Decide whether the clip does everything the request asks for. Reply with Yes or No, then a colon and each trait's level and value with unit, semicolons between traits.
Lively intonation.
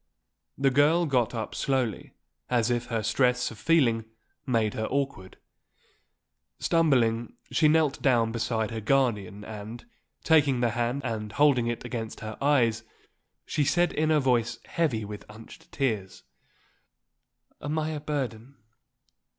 No: average, 4.2 semitones